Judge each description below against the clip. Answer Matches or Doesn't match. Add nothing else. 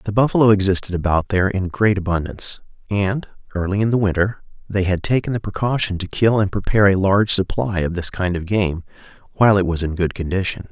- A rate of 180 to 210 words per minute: Matches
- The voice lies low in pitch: Matches